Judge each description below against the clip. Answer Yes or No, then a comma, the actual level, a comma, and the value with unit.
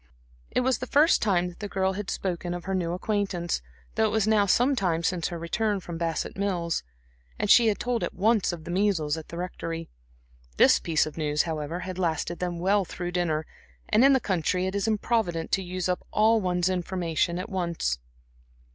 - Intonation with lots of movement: No, average, 3.3 semitones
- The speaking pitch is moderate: Yes, medium, 180 Hz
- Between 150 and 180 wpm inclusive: No, fast, 205 wpm